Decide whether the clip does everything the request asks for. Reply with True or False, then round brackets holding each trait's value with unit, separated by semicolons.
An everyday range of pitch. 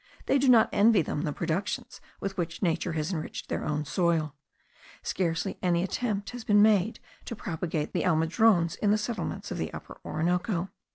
True (4.3 semitones)